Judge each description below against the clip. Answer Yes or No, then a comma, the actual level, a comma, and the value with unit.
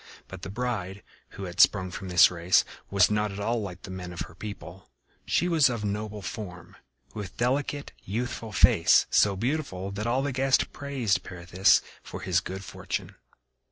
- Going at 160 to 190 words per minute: Yes, average, 175 wpm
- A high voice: No, low, 100 Hz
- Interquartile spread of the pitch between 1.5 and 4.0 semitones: No, average, 4.4 semitones